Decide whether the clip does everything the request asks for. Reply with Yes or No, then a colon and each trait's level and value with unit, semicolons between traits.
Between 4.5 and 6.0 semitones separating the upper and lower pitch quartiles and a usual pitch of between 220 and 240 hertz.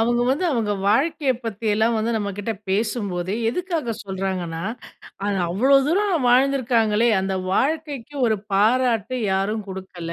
Yes: average, 4.8 semitones; high, 225 Hz